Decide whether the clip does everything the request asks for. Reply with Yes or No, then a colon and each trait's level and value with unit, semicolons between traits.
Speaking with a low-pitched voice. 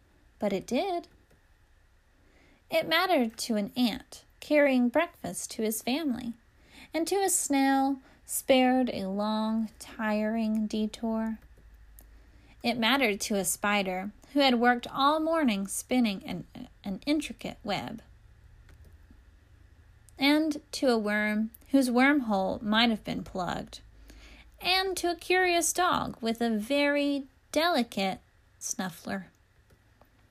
No: high, 235 Hz